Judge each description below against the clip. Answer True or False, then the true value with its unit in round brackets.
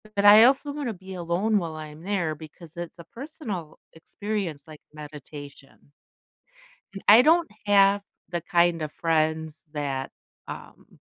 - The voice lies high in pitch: False (170 Hz)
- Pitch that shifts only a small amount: False (4.8 semitones)